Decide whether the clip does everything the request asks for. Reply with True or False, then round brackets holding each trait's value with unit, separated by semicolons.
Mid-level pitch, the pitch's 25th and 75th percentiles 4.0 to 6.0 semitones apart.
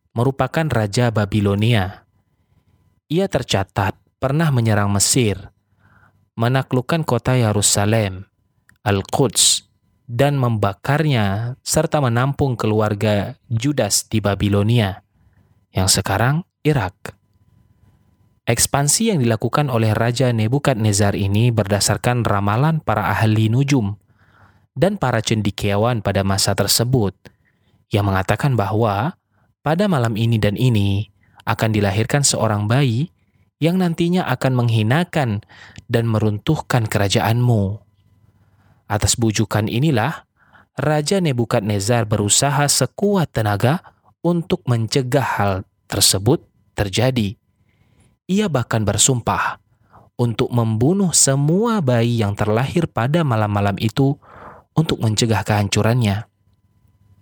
False (110 Hz; 4.3 semitones)